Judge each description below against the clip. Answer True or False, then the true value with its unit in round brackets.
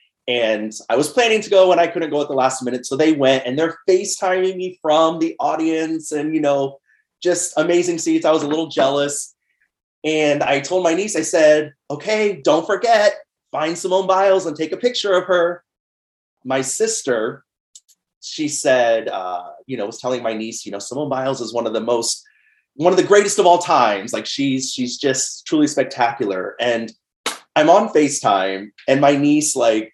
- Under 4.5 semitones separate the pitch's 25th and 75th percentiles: False (5.6 semitones)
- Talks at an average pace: True (190 wpm)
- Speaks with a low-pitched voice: False (155 Hz)